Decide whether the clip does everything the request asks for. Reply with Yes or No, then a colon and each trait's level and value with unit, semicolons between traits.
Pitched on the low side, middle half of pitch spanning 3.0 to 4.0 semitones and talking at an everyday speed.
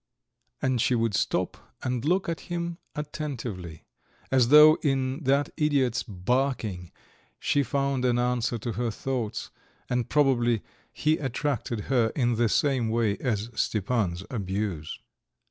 No: low, 125 Hz; average, 3.7 semitones; slow, 130 wpm